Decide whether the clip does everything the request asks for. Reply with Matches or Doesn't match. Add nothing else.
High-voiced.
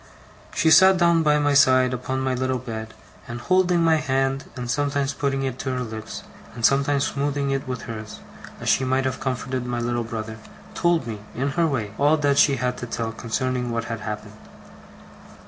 Doesn't match